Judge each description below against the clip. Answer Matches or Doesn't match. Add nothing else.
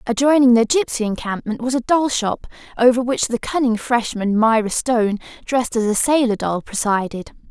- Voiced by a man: Doesn't match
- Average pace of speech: Matches